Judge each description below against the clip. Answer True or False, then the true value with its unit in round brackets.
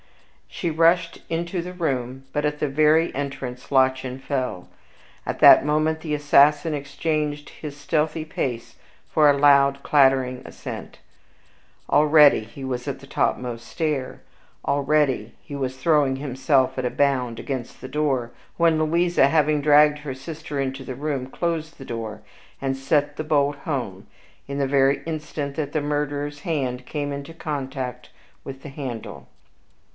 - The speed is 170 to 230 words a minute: False (150 wpm)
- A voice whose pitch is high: False (140 Hz)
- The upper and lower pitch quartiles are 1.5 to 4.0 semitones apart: True (2.4 semitones)